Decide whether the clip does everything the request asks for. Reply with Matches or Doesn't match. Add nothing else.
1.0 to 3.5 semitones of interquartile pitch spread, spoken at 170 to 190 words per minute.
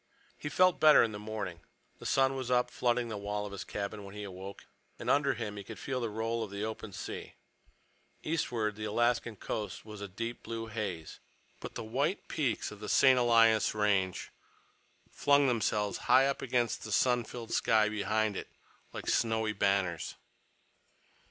Matches